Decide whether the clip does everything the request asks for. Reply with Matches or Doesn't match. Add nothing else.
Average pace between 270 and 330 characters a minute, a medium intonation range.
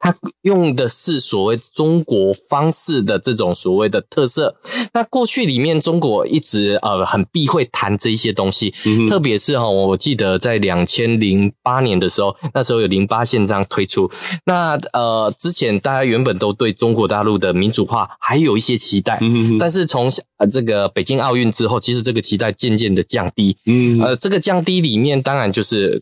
Doesn't match